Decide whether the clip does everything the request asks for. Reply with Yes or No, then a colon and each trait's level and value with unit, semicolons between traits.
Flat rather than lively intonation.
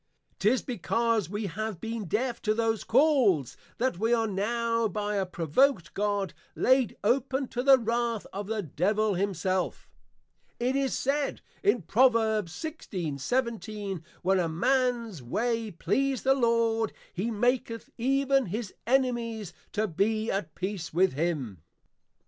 No: average, 4.1 semitones